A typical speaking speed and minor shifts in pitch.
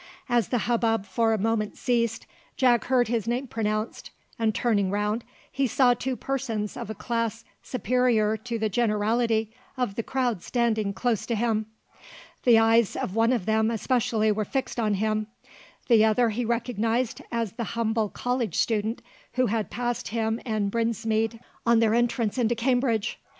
Yes: average, 165 wpm; narrow, 1.8 semitones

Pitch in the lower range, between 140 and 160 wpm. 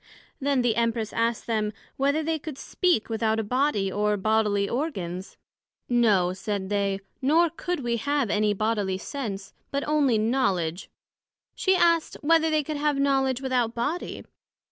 No: high, 235 Hz; average, 150 wpm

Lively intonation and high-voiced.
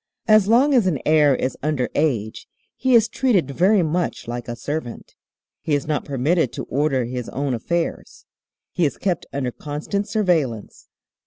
No: wide, 6.2 semitones; medium, 150 Hz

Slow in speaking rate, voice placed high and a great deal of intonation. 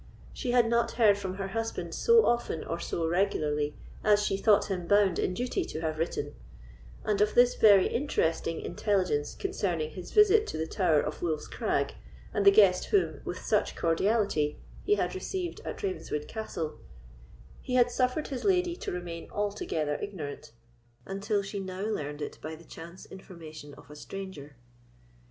No: average, 170 wpm; high, 195 Hz; wide, 5.9 semitones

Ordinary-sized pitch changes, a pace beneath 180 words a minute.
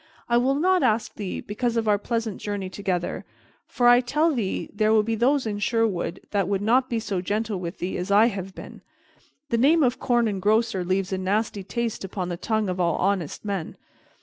No: average, 3.7 semitones; average, 200 wpm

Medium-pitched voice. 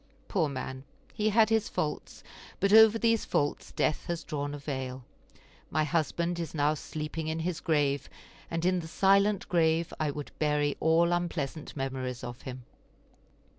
Yes: medium, 160 Hz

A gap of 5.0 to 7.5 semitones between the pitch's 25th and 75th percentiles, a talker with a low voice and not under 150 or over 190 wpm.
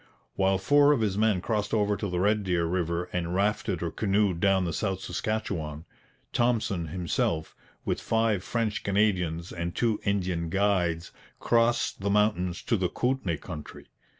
No: average, 3.6 semitones; very low, 95 Hz; average, 155 wpm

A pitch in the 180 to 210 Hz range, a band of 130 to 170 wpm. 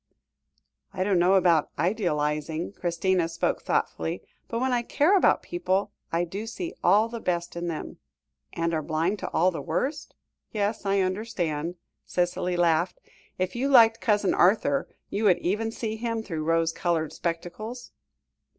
Yes: medium, 185 Hz; average, 160 wpm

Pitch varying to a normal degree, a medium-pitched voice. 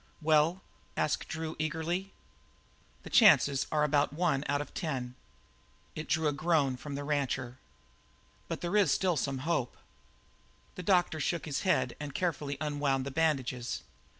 Yes: average, 3.0 semitones; medium, 150 Hz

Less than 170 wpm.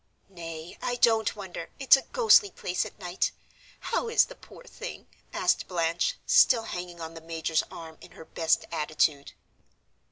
Yes: average, 160 wpm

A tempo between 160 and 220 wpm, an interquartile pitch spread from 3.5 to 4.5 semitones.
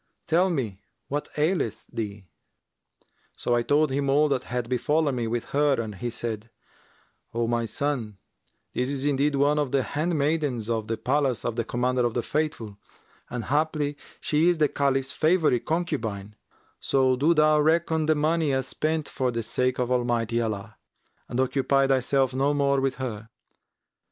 Yes: average, 165 wpm; average, 4.0 semitones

